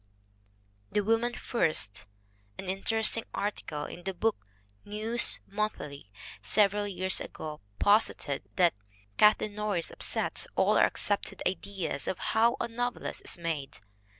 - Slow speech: Yes, slow, 125 wpm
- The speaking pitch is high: Yes, high, 205 Hz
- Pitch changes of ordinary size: Yes, average, 4.3 semitones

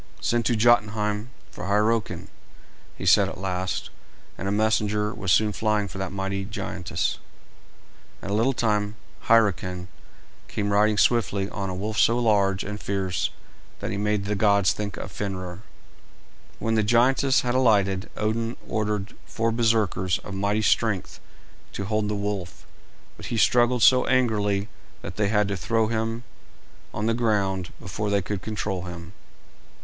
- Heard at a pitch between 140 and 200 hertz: No, low, 105 Hz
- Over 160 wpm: No, average, 155 wpm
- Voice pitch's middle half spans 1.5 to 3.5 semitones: Yes, narrow, 2.4 semitones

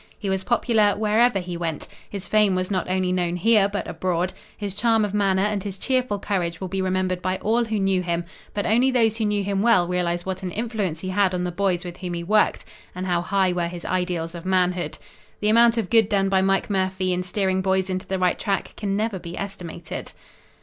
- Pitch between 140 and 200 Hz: Yes, high, 190 Hz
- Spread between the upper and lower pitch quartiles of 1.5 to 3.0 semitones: Yes, narrow, 2.5 semitones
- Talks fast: Yes, fast, 225 wpm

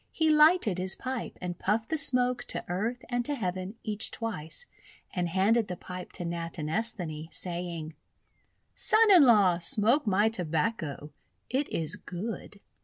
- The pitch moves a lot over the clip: Yes, wide, 5.7 semitones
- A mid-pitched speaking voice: No, high, 200 Hz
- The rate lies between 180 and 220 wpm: No, average, 155 wpm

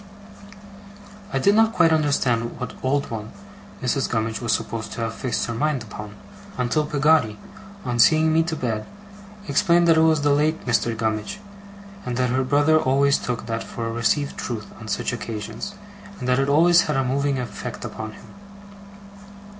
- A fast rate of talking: No, average, 175 wpm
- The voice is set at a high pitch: No, low, 130 Hz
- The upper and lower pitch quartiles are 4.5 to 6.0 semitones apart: Yes, average, 4.9 semitones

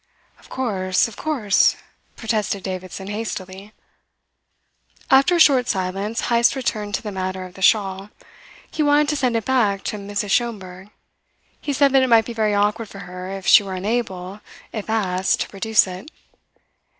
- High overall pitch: Yes, high, 210 Hz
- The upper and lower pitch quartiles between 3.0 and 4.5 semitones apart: Yes, average, 3.7 semitones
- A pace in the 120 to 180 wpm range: Yes, average, 165 wpm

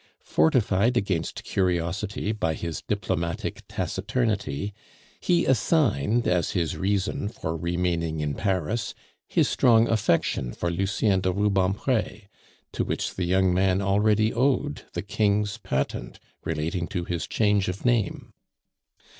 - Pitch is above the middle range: No, very low, 95 Hz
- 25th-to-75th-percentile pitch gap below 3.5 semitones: No, average, 3.8 semitones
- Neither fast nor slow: No, slow, 120 wpm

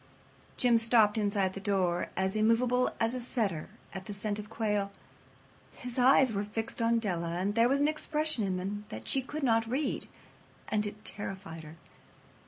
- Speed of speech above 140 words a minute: Yes, average, 180 wpm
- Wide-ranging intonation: No, average, 3.5 semitones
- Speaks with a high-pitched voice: Yes, high, 215 Hz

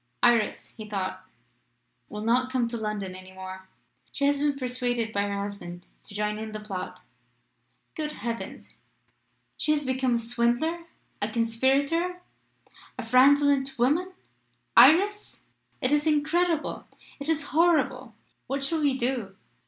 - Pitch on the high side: Yes, very high, 255 Hz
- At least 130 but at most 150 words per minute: Yes, slow, 135 wpm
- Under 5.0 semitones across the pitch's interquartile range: No, average, 5.3 semitones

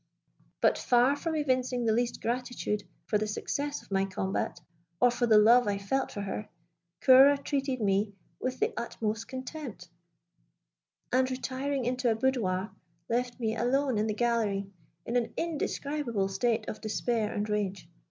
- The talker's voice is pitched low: No, high, 240 Hz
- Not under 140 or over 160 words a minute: Yes, average, 155 wpm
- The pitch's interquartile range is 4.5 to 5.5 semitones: No, average, 3.7 semitones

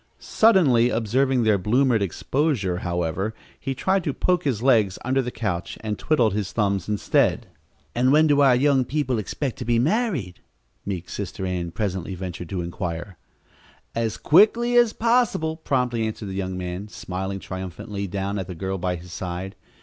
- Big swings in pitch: Yes, wide, 6.4 semitones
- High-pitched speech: No, low, 110 Hz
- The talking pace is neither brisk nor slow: Yes, average, 165 wpm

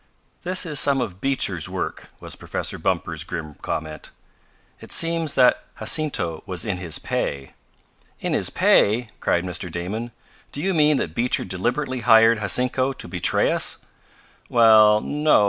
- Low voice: Yes, low, 115 Hz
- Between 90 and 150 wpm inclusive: Yes, average, 145 wpm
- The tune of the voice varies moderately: No, wide, 7.4 semitones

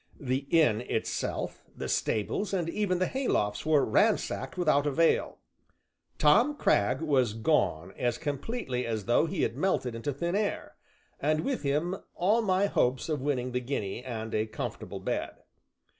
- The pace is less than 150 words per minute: No, average, 155 wpm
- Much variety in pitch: Yes, wide, 6.7 semitones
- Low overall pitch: No, medium, 145 Hz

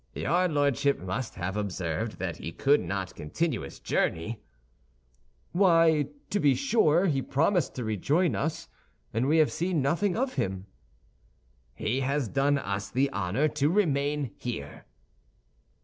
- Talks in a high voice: No, medium, 140 Hz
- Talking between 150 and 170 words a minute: No, average, 140 wpm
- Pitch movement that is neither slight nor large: No, wide, 7.5 semitones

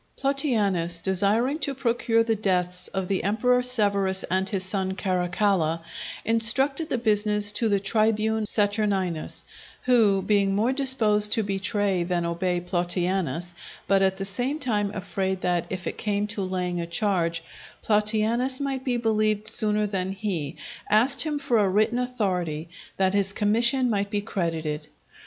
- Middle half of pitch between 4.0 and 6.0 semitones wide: No, average, 3.3 semitones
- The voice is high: Yes, high, 205 Hz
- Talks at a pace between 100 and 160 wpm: Yes, average, 150 wpm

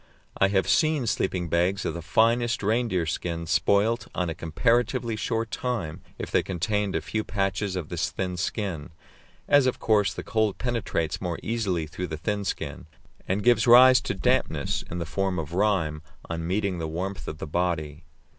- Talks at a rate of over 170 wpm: Yes, average, 180 wpm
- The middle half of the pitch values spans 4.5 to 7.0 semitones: Yes, average, 4.8 semitones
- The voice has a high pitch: No, very low, 95 Hz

